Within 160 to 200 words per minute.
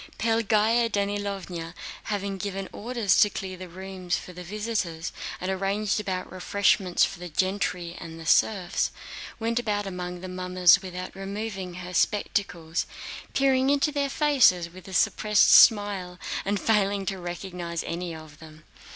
No: average, 145 wpm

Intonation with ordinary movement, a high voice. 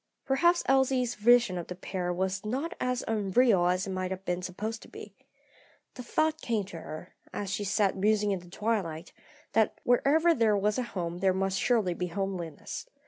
Yes: average, 4.8 semitones; high, 200 Hz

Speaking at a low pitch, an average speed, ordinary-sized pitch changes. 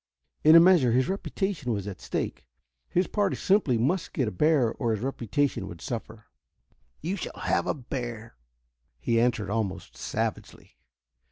No: low, 125 Hz; average, 155 wpm; wide, 6.5 semitones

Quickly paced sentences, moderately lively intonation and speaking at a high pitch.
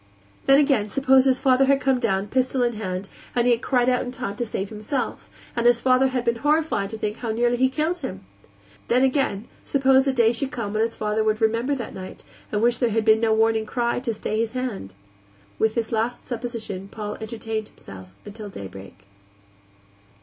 Yes: fast, 210 wpm; average, 3.0 semitones; high, 235 Hz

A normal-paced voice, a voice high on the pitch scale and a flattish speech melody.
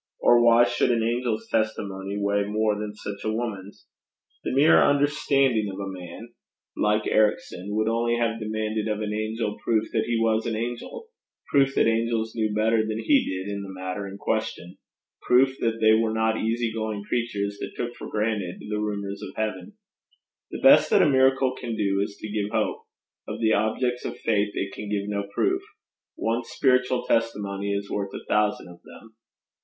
No: average, 185 wpm; low, 110 Hz; narrow, 2.3 semitones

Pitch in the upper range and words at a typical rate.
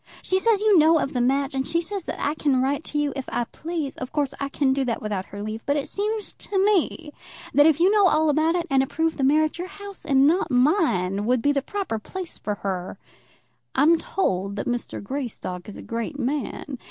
No: very high, 285 Hz; fast, 230 wpm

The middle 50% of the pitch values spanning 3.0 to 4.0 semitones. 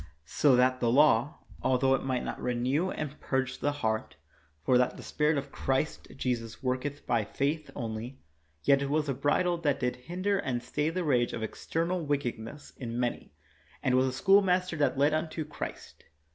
Yes: average, 3.6 semitones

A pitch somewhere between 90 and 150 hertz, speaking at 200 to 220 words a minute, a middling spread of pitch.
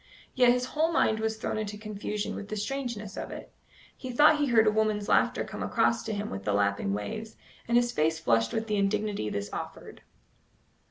No: high, 215 Hz; fast, 205 wpm; average, 3.3 semitones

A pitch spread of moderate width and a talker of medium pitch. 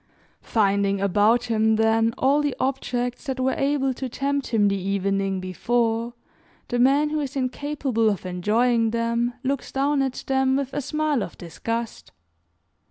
No: average, 3.8 semitones; high, 240 Hz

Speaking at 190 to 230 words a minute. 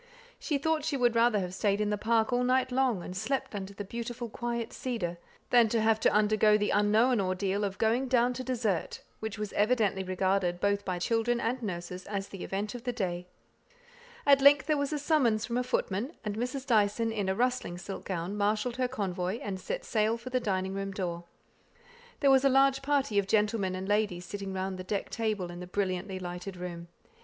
Yes: fast, 205 wpm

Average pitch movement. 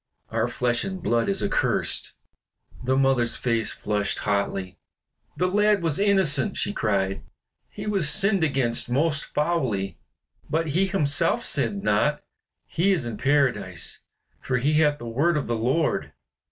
No: wide, 6.6 semitones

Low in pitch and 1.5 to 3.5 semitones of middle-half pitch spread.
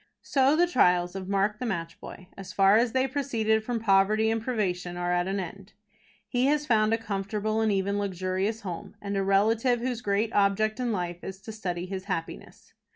No: high, 205 Hz; average, 2.9 semitones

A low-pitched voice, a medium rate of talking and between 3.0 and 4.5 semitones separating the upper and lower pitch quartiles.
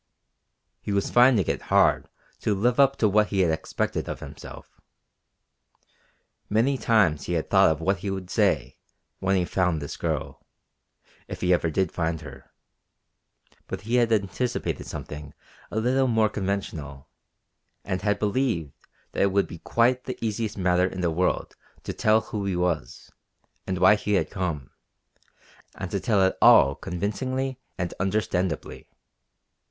Yes: very low, 95 Hz; average, 155 wpm; average, 3.7 semitones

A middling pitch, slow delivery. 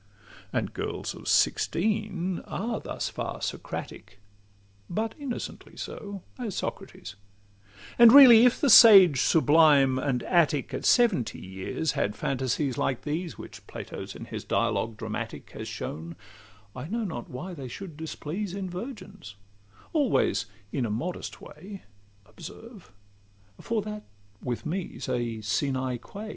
Yes: medium, 160 Hz; slow, 130 wpm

